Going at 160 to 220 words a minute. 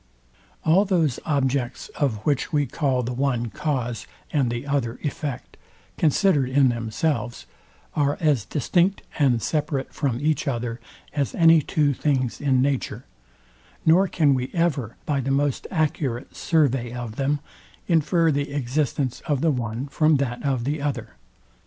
No: average, 145 wpm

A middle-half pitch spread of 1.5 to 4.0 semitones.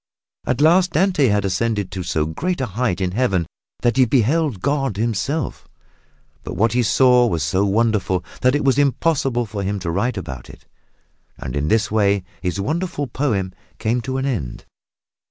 No: wide, 5.6 semitones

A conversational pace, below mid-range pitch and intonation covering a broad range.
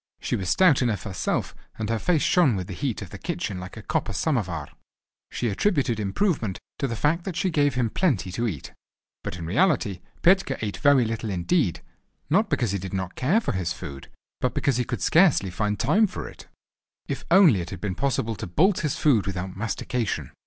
No: fast, 210 wpm; low, 115 Hz; wide, 8.2 semitones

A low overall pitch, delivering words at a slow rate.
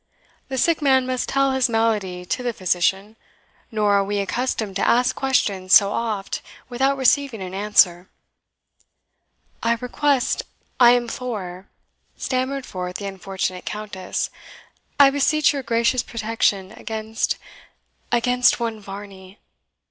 No: high, 225 Hz; slow, 125 wpm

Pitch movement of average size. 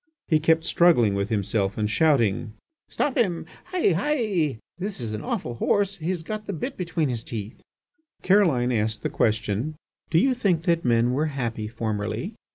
No: wide, 8.4 semitones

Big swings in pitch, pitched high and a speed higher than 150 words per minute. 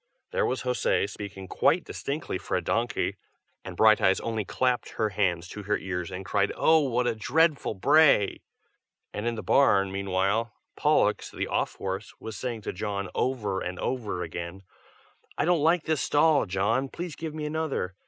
No: wide, 6.4 semitones; low, 110 Hz; average, 175 wpm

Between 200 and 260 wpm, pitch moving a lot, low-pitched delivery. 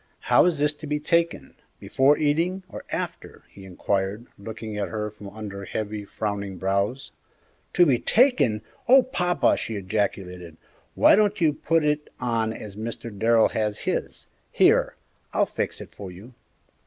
No: average, 155 wpm; wide, 6.7 semitones; low, 110 Hz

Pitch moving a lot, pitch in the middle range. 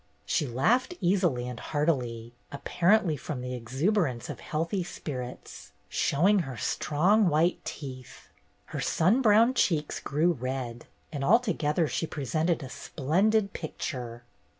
Yes: wide, 6.4 semitones; medium, 155 Hz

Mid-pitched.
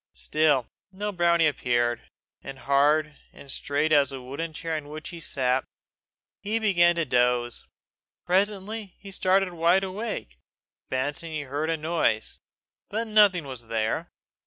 Yes: medium, 155 Hz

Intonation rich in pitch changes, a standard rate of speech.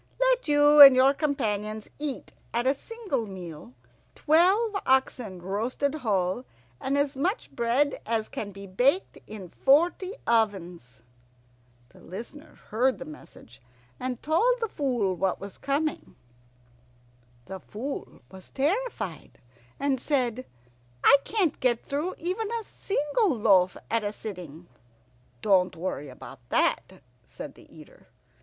No: wide, 7.0 semitones; slow, 130 wpm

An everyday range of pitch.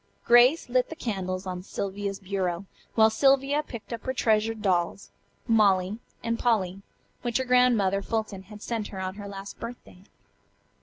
Yes: average, 3.8 semitones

